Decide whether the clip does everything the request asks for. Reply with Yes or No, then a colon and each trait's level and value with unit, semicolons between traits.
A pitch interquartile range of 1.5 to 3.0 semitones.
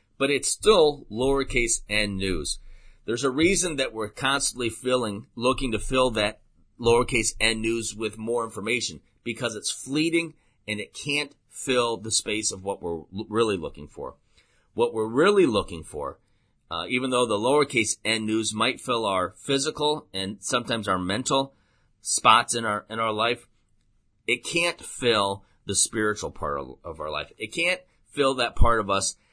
No: average, 3.7 semitones